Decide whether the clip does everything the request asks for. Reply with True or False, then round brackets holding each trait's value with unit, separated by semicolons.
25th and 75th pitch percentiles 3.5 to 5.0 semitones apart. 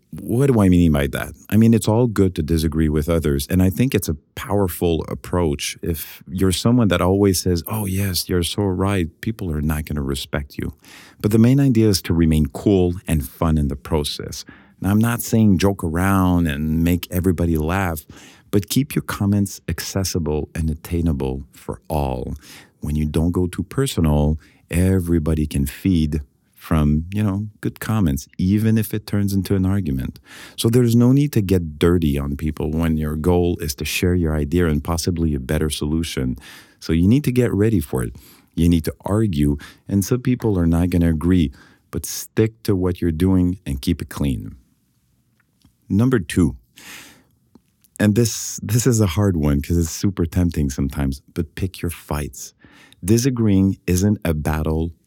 True (4.5 semitones)